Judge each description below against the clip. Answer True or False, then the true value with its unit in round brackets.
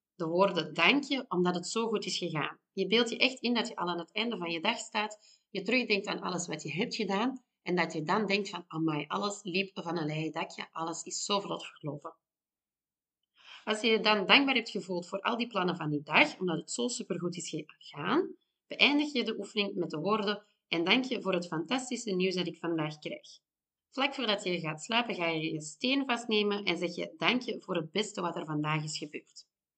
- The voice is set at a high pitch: True (195 Hz)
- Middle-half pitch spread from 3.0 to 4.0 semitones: False (4.9 semitones)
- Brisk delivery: True (230 wpm)